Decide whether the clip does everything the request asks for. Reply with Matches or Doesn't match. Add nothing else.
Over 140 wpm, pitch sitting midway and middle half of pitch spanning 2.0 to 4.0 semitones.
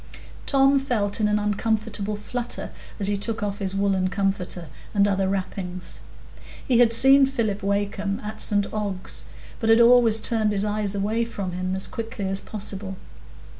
Doesn't match